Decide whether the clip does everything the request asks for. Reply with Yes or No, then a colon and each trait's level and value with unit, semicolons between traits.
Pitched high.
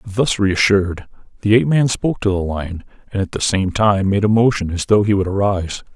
No: low, 100 Hz